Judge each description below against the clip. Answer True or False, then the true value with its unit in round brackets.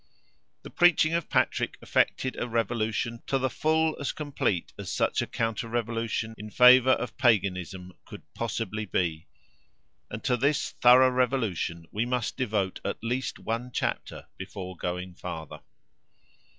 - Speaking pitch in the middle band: False (115 Hz)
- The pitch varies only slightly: False (4.2 semitones)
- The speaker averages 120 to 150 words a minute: True (140 wpm)